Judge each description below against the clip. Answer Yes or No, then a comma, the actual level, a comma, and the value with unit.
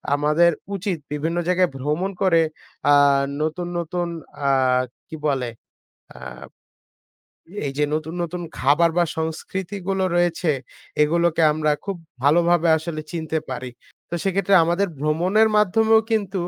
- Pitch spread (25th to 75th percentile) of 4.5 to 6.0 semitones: No, average, 3.2 semitones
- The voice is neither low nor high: Yes, medium, 170 Hz